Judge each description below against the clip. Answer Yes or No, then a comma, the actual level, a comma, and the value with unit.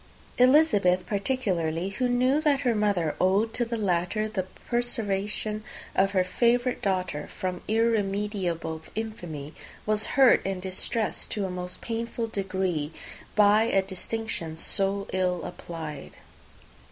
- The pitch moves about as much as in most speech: Yes, average, 3.8 semitones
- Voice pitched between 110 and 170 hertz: No, high, 200 Hz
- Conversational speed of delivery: No, slow, 125 wpm